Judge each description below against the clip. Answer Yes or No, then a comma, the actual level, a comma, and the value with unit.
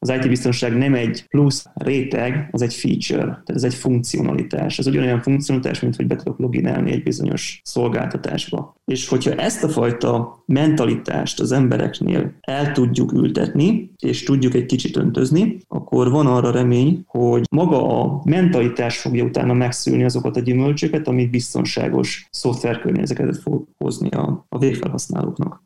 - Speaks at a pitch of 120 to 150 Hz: Yes, low, 125 Hz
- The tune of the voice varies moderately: Yes, average, 3.3 semitones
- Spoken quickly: No, average, 145 wpm